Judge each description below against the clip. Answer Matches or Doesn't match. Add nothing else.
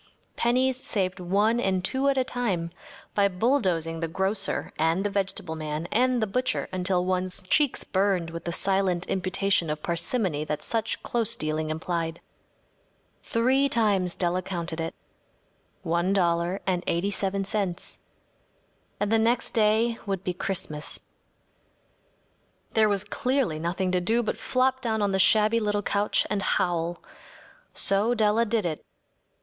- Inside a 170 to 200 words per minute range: Doesn't match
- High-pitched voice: Matches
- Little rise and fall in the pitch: Doesn't match